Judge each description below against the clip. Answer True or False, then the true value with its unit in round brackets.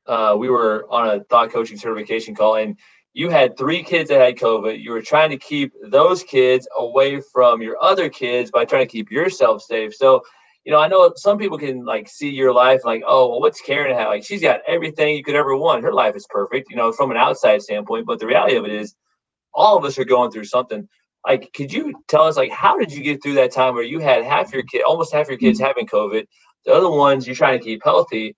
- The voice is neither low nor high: False (130 Hz)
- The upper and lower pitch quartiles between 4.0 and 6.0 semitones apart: True (5.1 semitones)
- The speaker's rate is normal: False (245 wpm)